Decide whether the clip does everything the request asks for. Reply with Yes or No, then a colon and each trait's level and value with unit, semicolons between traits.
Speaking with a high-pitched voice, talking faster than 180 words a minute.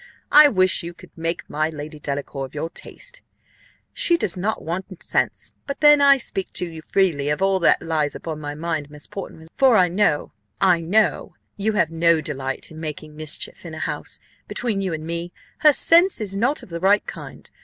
No: medium, 170 Hz; average, 200 wpm